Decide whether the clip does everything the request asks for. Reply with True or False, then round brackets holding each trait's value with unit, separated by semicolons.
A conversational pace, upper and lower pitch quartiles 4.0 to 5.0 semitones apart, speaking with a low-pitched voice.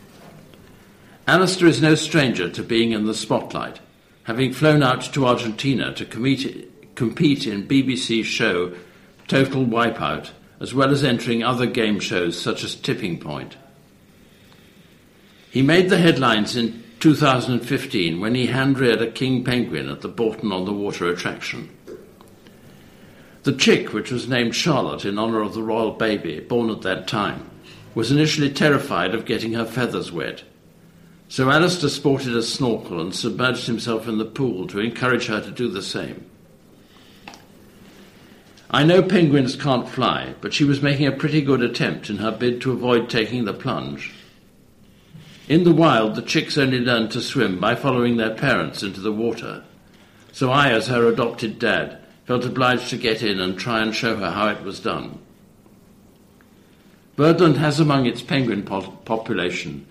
False (155 wpm; 3.6 semitones; 120 Hz)